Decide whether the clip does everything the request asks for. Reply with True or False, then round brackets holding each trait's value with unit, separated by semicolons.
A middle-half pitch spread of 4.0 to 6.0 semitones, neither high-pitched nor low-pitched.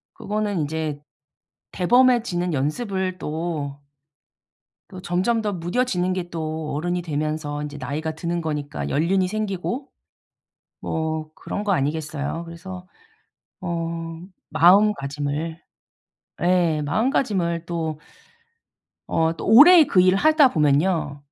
False (3.5 semitones; 170 Hz)